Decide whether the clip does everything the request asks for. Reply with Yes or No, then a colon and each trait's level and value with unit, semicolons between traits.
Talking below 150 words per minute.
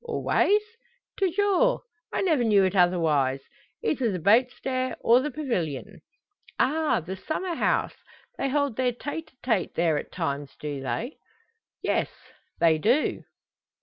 Yes: average, 140 wpm